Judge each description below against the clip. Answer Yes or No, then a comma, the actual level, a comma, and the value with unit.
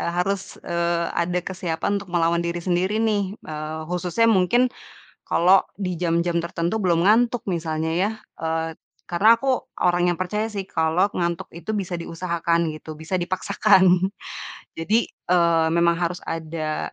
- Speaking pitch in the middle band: Yes, medium, 175 Hz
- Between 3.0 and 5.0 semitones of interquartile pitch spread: No, narrow, 2.4 semitones